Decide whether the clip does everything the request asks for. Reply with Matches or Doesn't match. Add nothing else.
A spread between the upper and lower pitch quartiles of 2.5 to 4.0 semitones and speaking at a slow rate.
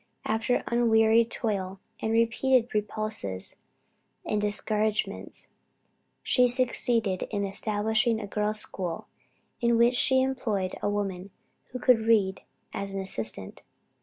Matches